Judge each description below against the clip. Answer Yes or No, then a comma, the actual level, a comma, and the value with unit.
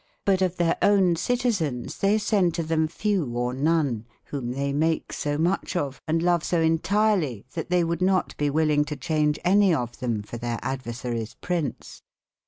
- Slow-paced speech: No, average, 180 wpm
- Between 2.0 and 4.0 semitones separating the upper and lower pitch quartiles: No, average, 5.1 semitones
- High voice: No, medium, 160 Hz